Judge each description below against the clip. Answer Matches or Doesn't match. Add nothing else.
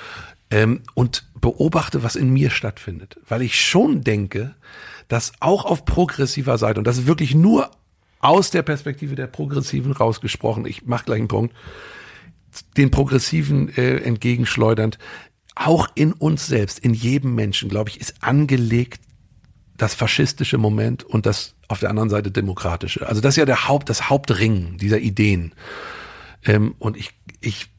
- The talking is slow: Doesn't match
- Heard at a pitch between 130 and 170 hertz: Doesn't match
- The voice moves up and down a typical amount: Matches